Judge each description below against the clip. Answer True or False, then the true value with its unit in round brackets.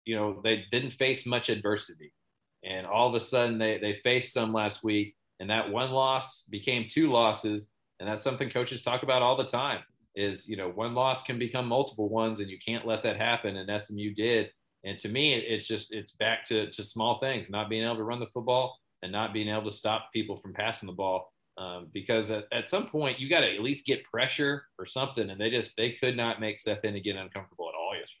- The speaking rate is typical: False (235 wpm)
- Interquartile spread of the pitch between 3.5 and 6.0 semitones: False (3.0 semitones)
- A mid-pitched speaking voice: False (110 Hz)